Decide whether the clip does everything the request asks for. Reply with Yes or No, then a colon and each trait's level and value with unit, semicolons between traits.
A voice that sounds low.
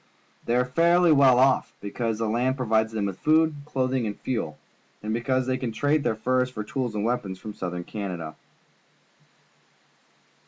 Yes: low, 120 Hz